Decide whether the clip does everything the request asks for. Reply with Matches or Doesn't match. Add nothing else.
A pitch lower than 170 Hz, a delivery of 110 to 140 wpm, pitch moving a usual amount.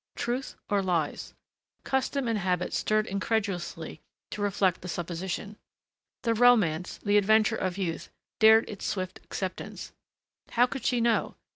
Doesn't match